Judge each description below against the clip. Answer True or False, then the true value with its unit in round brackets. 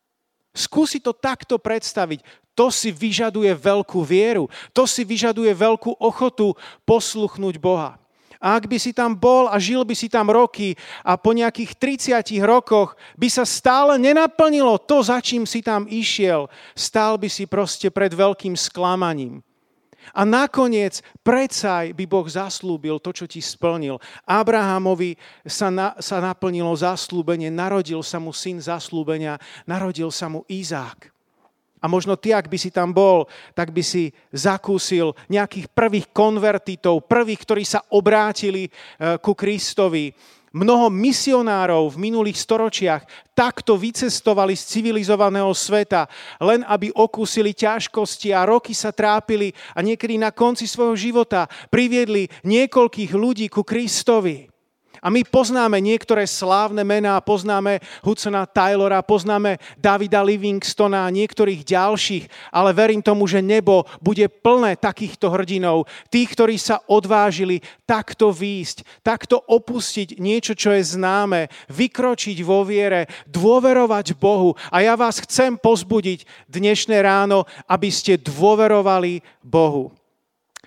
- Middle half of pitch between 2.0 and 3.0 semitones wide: False (3.5 semitones)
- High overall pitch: True (205 Hz)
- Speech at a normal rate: True (130 wpm)